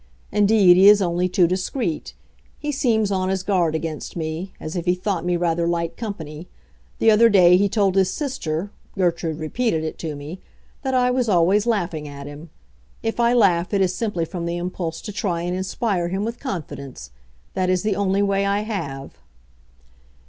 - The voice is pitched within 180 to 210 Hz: Yes, medium, 185 Hz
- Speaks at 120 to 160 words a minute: No, average, 180 wpm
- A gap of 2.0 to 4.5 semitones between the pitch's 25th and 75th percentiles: Yes, average, 3.6 semitones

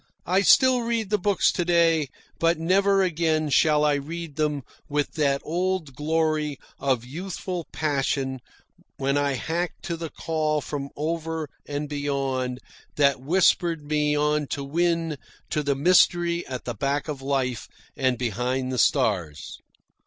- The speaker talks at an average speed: Yes, average, 145 wpm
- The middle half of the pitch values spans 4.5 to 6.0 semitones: No, average, 3.5 semitones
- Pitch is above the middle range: No, medium, 150 Hz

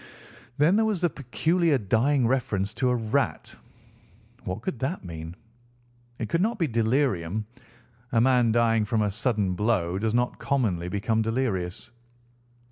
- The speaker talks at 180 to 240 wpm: No, average, 145 wpm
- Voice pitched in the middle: No, low, 115 Hz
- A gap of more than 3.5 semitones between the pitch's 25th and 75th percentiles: Yes, average, 4.5 semitones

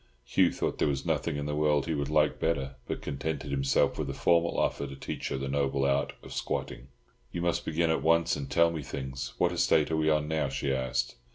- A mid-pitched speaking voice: No, very low, 75 Hz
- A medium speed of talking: No, fast, 235 wpm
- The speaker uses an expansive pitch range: No, average, 2.8 semitones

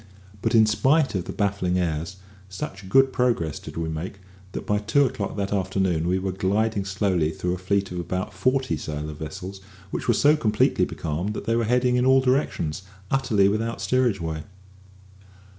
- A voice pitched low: Yes, low, 100 Hz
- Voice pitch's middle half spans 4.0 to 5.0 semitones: Yes, average, 4.4 semitones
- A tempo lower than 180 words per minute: No, average, 185 wpm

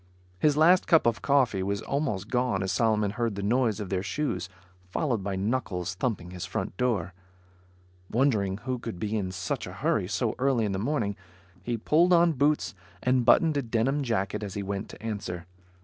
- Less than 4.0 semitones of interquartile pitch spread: No, average, 5.1 semitones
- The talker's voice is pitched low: Yes, low, 110 Hz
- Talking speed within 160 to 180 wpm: No, average, 190 wpm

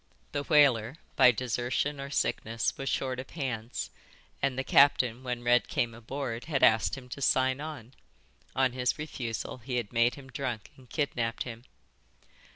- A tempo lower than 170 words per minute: Yes, average, 160 wpm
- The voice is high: No, low, 125 Hz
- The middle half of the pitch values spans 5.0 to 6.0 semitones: No, narrow, 2.6 semitones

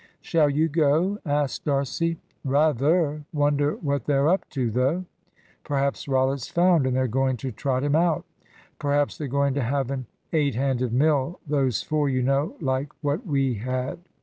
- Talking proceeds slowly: No, average, 165 wpm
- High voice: No, medium, 140 Hz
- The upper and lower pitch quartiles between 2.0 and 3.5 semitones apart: Yes, narrow, 2.5 semitones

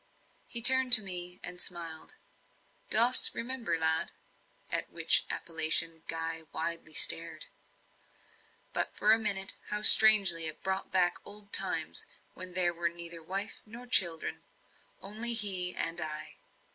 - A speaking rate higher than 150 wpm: No, slow, 135 wpm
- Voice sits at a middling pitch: Yes, medium, 180 Hz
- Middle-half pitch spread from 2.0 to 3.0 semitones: No, average, 4.3 semitones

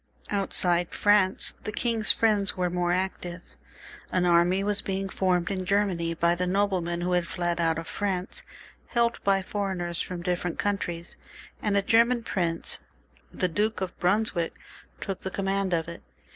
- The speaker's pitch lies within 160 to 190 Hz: Yes, medium, 185 Hz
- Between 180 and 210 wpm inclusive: No, average, 160 wpm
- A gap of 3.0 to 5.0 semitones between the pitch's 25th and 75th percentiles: No, narrow, 2.5 semitones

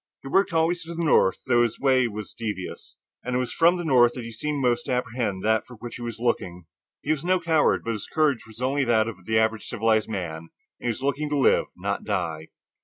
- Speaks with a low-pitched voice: Yes, low, 120 Hz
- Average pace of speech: No, fast, 245 wpm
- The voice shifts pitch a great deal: No, average, 4.4 semitones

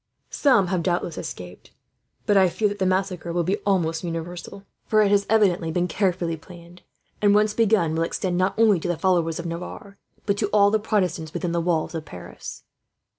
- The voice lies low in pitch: No, medium, 180 Hz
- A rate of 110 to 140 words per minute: No, average, 195 wpm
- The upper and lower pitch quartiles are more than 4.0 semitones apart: No, average, 3.2 semitones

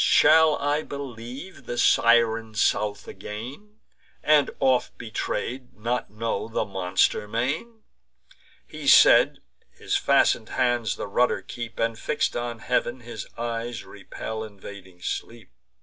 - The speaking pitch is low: Yes, low, 115 Hz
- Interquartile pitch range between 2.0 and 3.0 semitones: Yes, average, 2.7 semitones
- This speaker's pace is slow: Yes, slow, 120 wpm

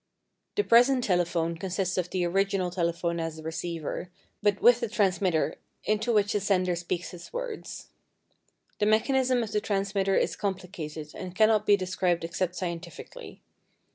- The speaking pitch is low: No, medium, 185 Hz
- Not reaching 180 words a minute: Yes, average, 150 wpm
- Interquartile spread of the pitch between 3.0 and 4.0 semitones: Yes, average, 3.4 semitones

